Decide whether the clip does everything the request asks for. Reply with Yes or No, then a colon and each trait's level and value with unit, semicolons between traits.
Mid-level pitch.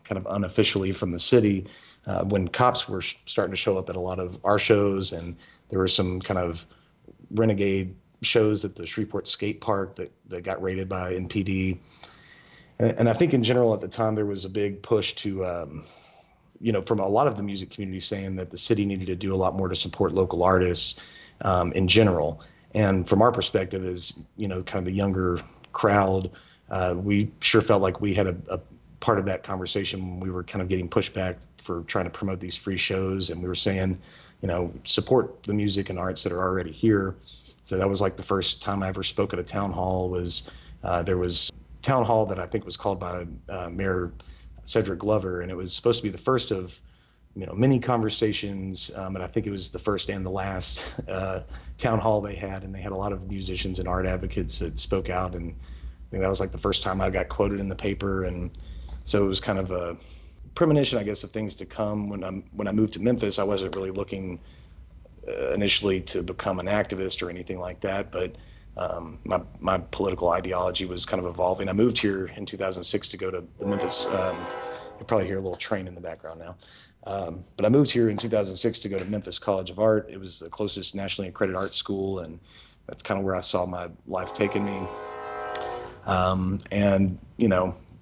No: very low, 95 Hz